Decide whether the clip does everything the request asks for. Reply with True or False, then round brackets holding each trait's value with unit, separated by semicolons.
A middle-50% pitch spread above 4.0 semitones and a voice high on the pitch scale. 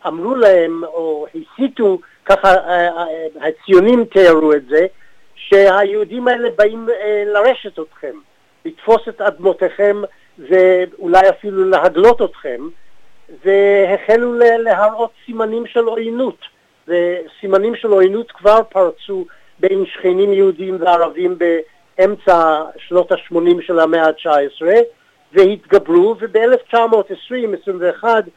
True (4.4 semitones; 195 Hz)